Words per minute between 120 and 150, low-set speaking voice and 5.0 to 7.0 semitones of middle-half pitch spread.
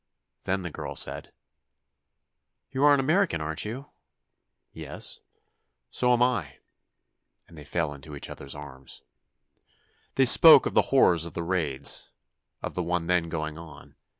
Yes: average, 145 wpm; very low, 85 Hz; average, 5.3 semitones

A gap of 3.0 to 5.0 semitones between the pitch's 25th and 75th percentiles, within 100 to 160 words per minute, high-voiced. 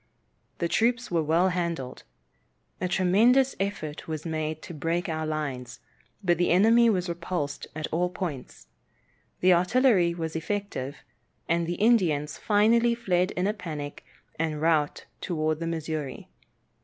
No: average, 3.5 semitones; average, 140 wpm; medium, 170 Hz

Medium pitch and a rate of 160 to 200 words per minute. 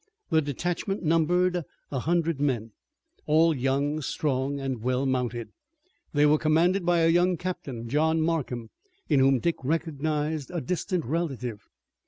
No: medium, 155 Hz; average, 140 wpm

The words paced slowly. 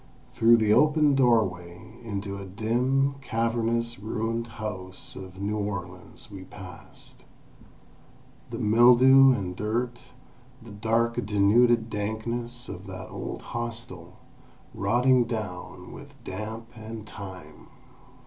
Yes: slow, 110 wpm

